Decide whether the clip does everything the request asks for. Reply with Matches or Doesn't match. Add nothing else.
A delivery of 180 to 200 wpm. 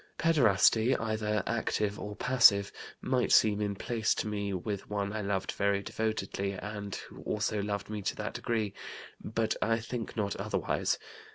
Doesn't match